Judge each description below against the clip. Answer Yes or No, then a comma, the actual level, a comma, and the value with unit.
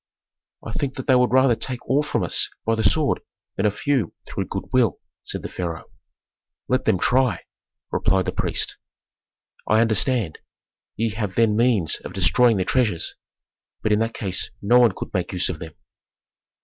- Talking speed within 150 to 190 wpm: Yes, average, 175 wpm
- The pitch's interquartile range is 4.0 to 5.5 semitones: Yes, average, 4.5 semitones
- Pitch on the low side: Yes, low, 110 Hz